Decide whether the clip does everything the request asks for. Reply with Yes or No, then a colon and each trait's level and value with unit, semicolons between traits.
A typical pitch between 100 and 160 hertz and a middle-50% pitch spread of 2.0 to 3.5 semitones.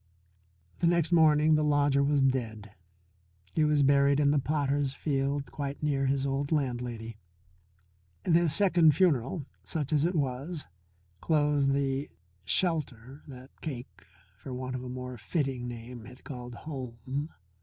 Yes: medium, 140 Hz; average, 2.8 semitones